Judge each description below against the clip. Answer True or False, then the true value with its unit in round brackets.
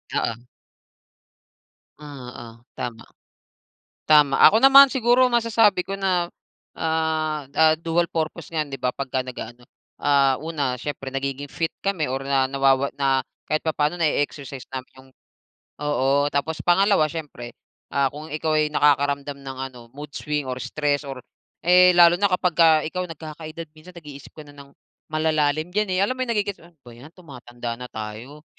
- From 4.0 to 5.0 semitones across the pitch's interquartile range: False (3.5 semitones)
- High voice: False (150 Hz)